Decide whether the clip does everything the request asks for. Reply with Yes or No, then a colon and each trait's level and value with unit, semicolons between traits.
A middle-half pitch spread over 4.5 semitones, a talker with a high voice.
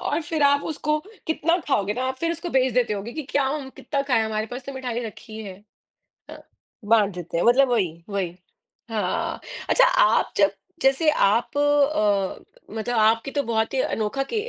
Yes: average, 5.1 semitones; very high, 250 Hz